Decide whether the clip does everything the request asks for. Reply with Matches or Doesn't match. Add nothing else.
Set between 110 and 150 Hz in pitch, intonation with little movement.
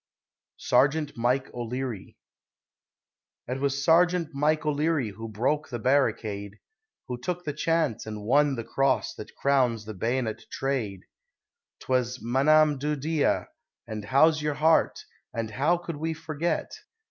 Doesn't match